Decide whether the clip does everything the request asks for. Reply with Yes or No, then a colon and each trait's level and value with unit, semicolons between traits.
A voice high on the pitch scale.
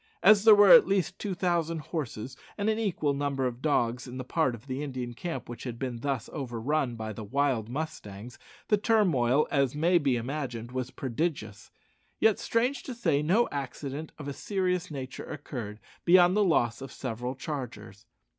No: medium, 140 Hz